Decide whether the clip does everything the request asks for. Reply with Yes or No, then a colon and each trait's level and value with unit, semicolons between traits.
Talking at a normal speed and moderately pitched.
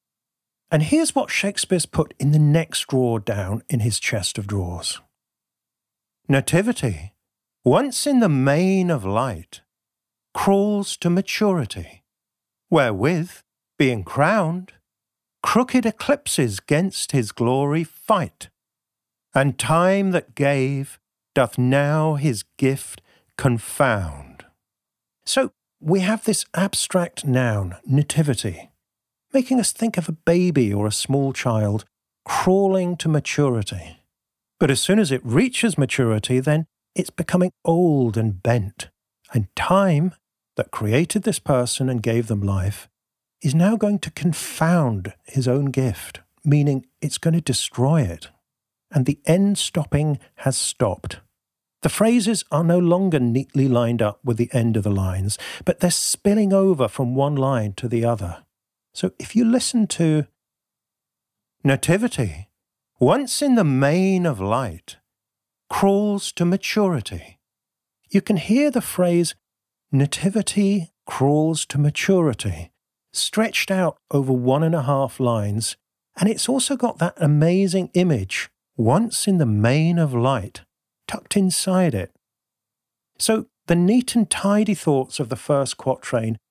No: slow, 130 wpm; medium, 145 Hz